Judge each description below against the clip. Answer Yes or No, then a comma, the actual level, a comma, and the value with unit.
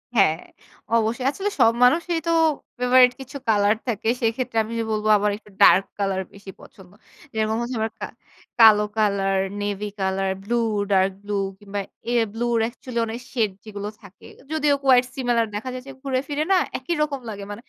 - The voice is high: Yes, high, 225 Hz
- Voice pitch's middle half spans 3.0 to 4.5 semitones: Yes, average, 3.8 semitones